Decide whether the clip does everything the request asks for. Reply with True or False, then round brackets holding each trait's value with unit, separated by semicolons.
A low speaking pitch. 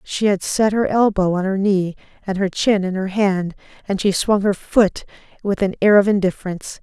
False (195 Hz)